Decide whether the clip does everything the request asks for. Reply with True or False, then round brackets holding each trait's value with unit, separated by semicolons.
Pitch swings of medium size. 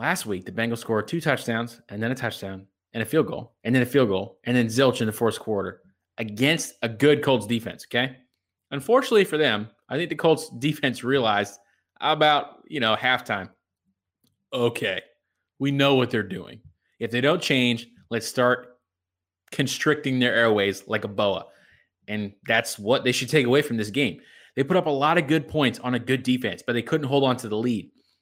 True (3.8 semitones)